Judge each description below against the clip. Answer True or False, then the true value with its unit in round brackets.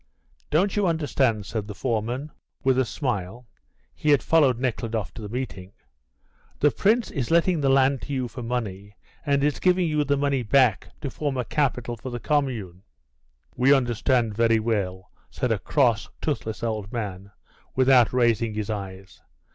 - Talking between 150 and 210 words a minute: True (165 wpm)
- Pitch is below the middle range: True (125 Hz)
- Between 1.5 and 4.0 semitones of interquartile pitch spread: False (4.5 semitones)